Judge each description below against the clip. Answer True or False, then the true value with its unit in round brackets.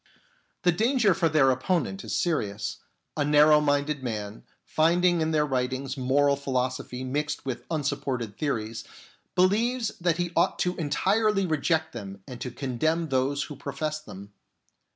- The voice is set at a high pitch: False (145 Hz)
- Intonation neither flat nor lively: True (4.6 semitones)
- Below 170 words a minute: True (145 wpm)